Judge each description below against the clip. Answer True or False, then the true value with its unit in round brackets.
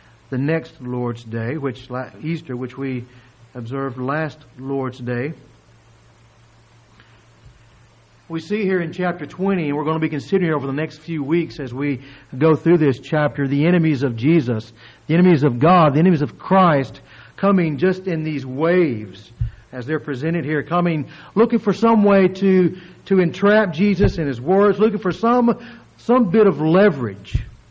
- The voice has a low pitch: False (150 Hz)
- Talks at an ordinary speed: True (160 wpm)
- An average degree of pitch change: False (6.3 semitones)